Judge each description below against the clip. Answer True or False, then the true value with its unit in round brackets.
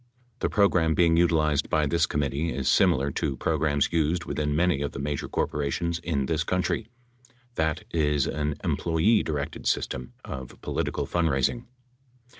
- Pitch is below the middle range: True (75 Hz)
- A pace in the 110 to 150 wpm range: True (145 wpm)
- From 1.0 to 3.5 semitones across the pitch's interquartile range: True (2.9 semitones)